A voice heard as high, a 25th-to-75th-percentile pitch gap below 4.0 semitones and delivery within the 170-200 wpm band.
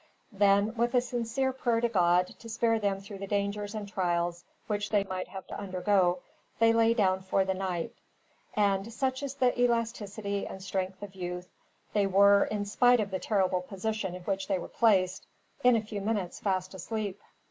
Yes: high, 200 Hz; average, 3.1 semitones; average, 190 wpm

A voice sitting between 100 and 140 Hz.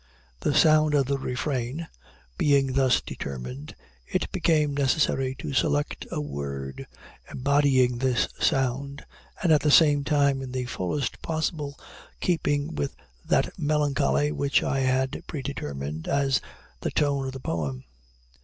Yes: low, 135 Hz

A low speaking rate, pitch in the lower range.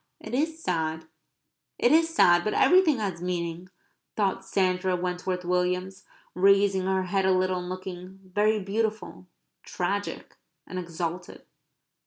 No: slow, 130 wpm; medium, 185 Hz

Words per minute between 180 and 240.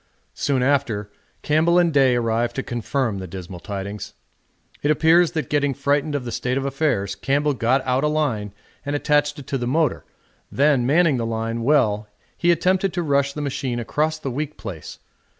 Yes: average, 185 wpm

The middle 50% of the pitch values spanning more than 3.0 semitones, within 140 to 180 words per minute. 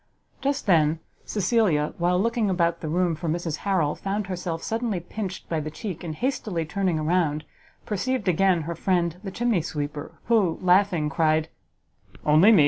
Yes: average, 4.0 semitones; average, 160 wpm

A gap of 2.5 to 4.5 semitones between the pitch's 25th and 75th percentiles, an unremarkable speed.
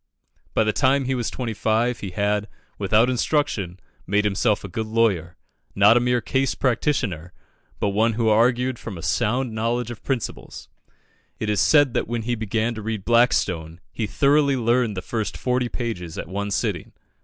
Yes: average, 3.2 semitones; average, 180 wpm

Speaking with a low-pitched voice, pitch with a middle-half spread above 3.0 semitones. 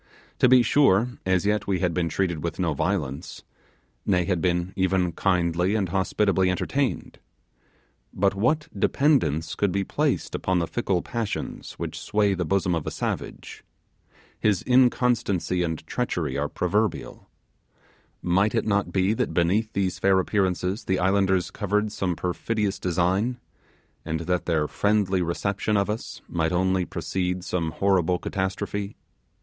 No: very low, 95 Hz; average, 2.7 semitones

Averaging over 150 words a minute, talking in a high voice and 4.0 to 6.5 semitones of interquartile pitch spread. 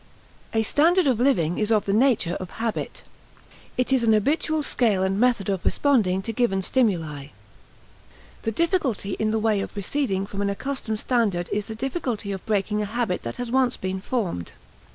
Yes: average, 180 wpm; high, 220 Hz; average, 4.3 semitones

